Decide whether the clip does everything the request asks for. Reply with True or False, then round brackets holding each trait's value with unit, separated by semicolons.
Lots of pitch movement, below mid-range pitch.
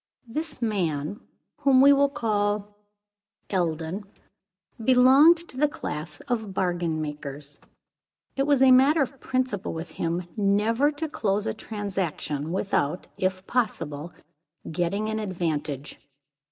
False (7.4 semitones; 205 Hz)